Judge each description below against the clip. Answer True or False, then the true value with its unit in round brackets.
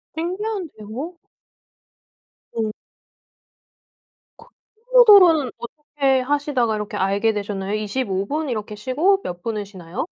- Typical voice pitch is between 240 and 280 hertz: True (245 Hz)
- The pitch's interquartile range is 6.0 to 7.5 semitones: True (7.1 semitones)